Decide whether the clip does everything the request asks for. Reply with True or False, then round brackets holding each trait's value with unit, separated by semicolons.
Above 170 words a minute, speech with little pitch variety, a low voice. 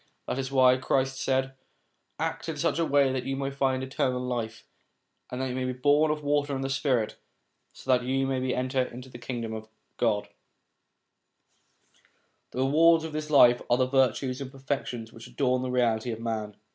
True (190 wpm; 1.6 semitones; 130 Hz)